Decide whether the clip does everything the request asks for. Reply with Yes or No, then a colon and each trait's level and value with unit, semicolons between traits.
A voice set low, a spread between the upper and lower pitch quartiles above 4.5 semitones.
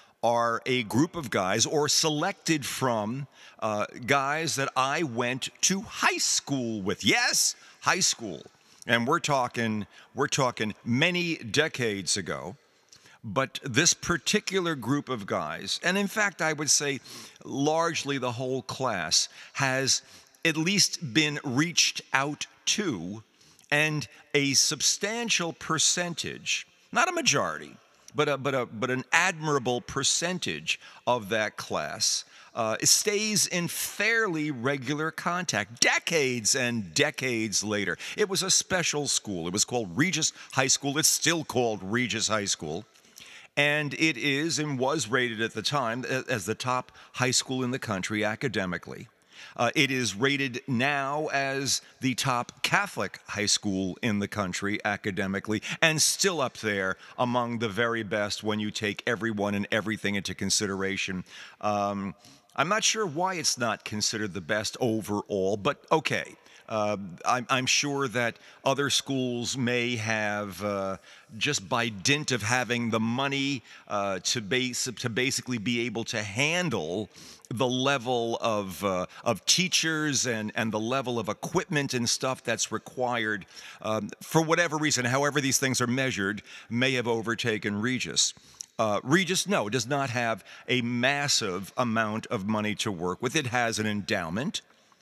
Yes: low, 125 Hz; average, 5.2 semitones